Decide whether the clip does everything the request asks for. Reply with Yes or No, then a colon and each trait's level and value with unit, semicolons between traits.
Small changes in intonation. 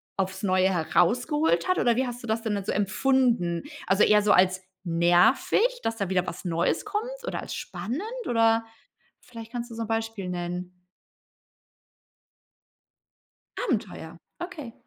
No: average, 5.0 semitones